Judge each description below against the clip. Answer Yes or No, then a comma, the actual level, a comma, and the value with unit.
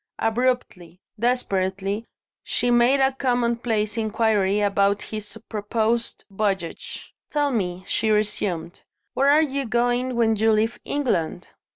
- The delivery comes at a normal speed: No, slow, 115 wpm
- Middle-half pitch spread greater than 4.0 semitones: No, average, 3.3 semitones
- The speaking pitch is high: Yes, high, 220 Hz